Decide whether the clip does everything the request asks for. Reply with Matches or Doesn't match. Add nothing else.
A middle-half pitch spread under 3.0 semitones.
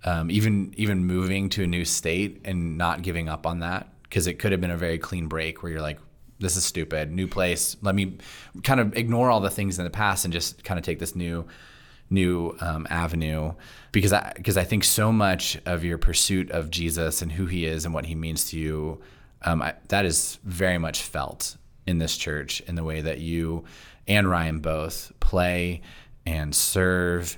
Matches